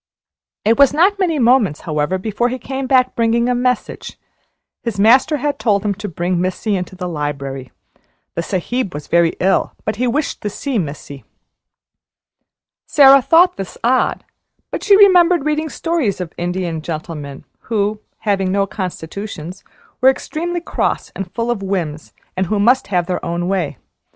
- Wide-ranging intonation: Yes, wide, 6.6 semitones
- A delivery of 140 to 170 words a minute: Yes, average, 160 wpm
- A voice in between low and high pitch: No, high, 205 Hz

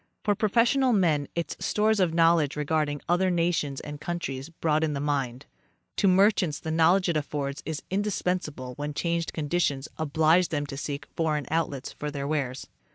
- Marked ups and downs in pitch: No, average, 3.3 semitones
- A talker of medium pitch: Yes, medium, 155 Hz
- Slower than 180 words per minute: Yes, average, 160 wpm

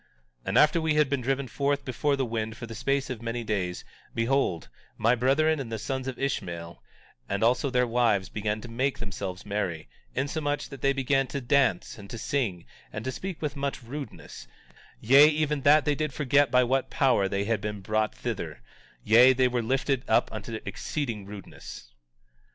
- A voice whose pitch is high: No, low, 125 Hz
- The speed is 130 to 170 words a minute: No, average, 190 wpm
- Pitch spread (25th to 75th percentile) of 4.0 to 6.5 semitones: Yes, average, 4.4 semitones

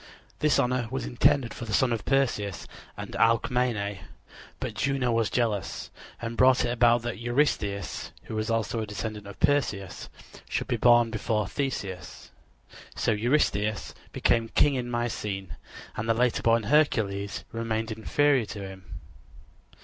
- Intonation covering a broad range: No, average, 2.9 semitones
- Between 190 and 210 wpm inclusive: No, average, 145 wpm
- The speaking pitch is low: Yes, low, 115 Hz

